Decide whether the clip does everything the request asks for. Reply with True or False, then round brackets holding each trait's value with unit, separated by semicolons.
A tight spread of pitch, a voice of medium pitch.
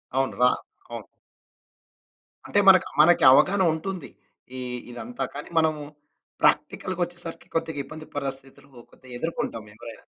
False (4.6 semitones; 155 Hz)